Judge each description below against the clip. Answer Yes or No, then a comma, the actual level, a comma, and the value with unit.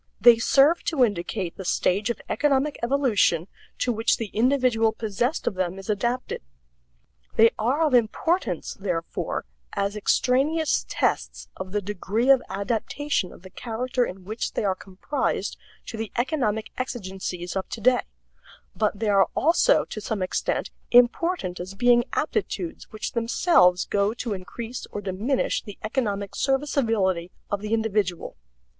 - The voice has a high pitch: Yes, high, 220 Hz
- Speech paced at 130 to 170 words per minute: Yes, average, 145 wpm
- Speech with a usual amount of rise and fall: Yes, average, 4.5 semitones